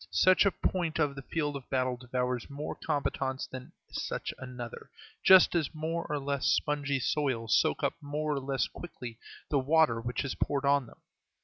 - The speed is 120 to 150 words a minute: No, average, 180 wpm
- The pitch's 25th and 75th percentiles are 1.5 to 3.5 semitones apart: Yes, average, 3.0 semitones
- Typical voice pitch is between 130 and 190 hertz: Yes, medium, 140 Hz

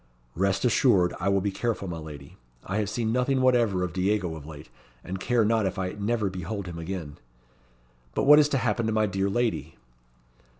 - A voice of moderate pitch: No, low, 100 Hz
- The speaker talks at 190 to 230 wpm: Yes, average, 200 wpm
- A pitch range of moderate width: Yes, average, 4.1 semitones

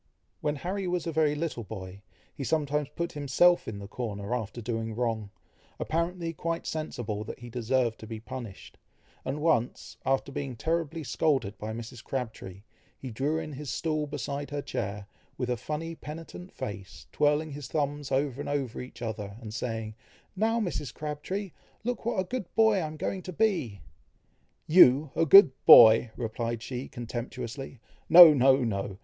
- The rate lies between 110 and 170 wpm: Yes, average, 165 wpm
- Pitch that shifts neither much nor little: No, wide, 5.7 semitones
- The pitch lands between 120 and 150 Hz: Yes, low, 135 Hz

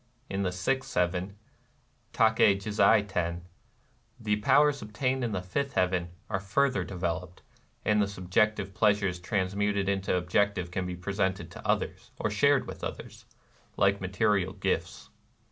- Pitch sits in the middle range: No, low, 100 Hz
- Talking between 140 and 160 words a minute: Yes, average, 145 wpm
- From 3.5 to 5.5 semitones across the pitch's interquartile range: No, narrow, 2.5 semitones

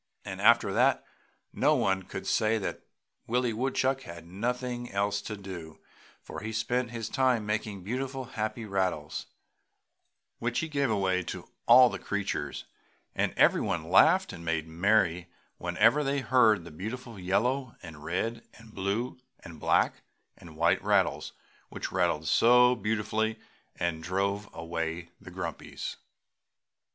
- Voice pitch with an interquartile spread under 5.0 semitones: No, average, 5.3 semitones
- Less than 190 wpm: Yes, average, 140 wpm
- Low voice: Yes, low, 105 Hz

